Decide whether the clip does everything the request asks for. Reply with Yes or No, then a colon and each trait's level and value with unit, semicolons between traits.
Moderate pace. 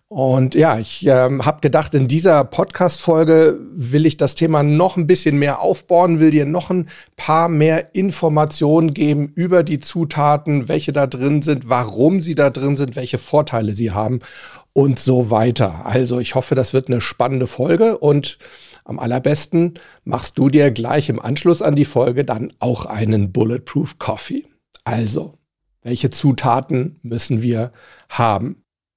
Yes: average, 160 wpm